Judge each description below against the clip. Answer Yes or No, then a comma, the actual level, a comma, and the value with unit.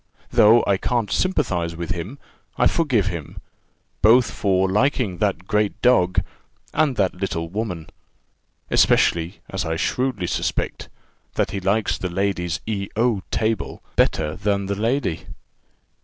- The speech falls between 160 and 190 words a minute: No, slow, 135 wpm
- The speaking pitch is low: Yes, low, 100 Hz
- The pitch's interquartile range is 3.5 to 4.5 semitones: Yes, average, 3.9 semitones